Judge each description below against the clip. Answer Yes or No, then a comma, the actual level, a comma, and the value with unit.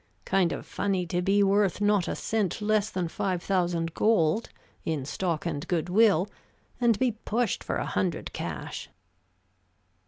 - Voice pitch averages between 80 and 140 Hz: No, high, 190 Hz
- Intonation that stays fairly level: No, average, 3.3 semitones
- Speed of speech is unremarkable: Yes, average, 155 wpm